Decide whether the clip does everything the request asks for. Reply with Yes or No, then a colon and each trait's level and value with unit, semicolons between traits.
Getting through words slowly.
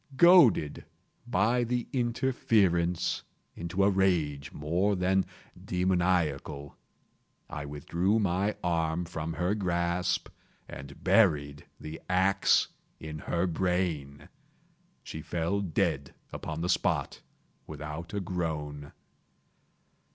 Yes: slow, 100 wpm